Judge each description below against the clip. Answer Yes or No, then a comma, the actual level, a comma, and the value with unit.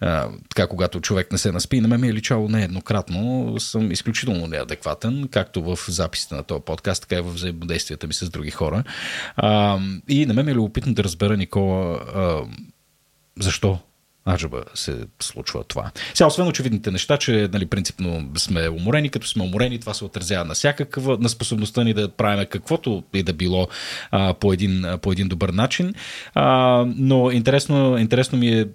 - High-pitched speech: No, low, 105 Hz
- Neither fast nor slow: No, fast, 175 wpm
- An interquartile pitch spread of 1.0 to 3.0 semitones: No, average, 4.7 semitones